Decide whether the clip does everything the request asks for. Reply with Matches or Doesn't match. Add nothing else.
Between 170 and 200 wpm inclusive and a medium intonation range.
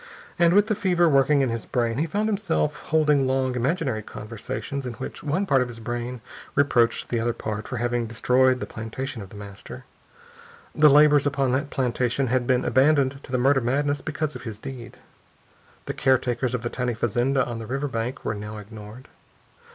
Matches